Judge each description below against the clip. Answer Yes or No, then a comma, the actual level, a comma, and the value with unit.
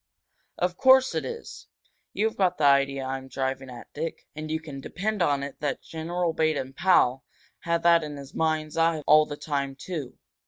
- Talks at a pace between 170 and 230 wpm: Yes, average, 185 wpm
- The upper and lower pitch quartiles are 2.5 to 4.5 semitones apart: Yes, average, 3.6 semitones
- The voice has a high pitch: No, medium, 155 Hz